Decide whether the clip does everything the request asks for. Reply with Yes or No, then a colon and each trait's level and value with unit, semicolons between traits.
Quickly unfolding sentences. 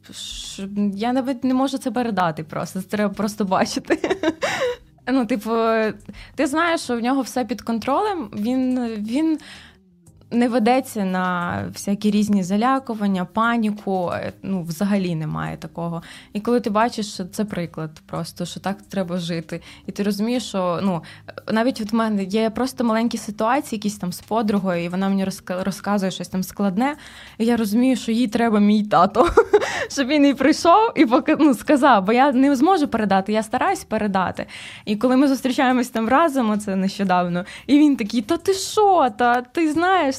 Yes: fast, 165 wpm